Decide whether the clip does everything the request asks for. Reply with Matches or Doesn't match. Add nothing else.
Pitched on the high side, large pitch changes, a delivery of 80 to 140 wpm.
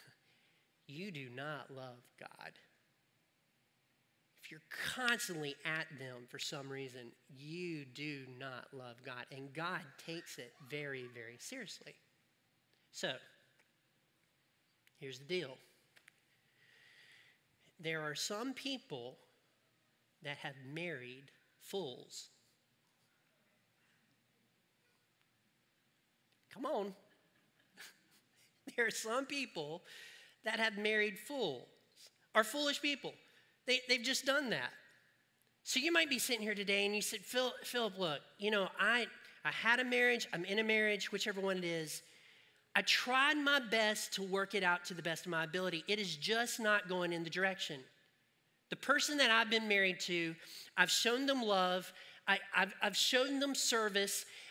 Matches